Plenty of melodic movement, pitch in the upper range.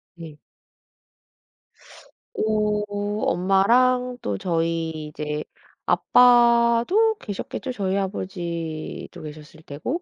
Yes: wide, 6.6 semitones; high, 195 Hz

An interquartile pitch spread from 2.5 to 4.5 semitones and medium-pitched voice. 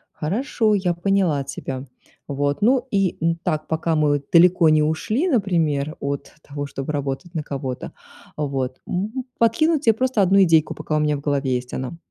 No: wide, 5.6 semitones; medium, 160 Hz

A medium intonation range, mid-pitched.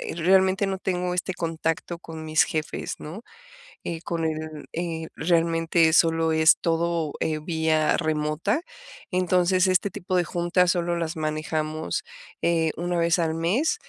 No: narrow, 2.0 semitones; medium, 165 Hz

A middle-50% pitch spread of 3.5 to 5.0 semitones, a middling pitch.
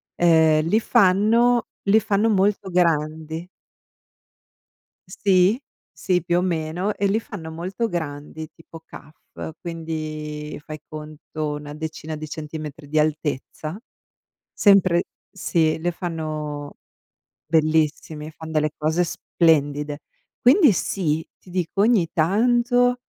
Yes: average, 3.8 semitones; medium, 160 Hz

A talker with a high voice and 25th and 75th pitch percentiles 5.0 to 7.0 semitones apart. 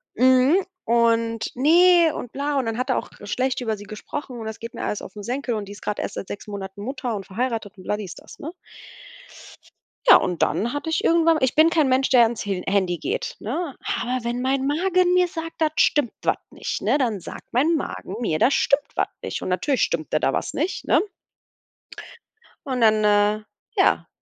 Yes: high, 245 Hz; wide, 5.4 semitones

